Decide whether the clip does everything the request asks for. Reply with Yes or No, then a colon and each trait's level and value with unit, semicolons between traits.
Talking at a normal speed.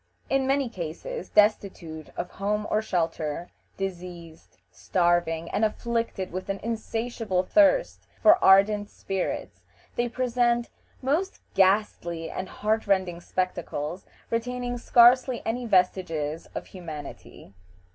No: slow, 110 wpm